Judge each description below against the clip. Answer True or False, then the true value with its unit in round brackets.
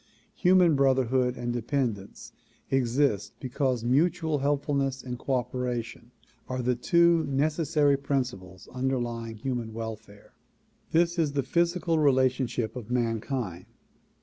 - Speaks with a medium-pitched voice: False (130 Hz)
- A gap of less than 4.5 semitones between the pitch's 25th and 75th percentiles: True (3.3 semitones)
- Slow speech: True (110 wpm)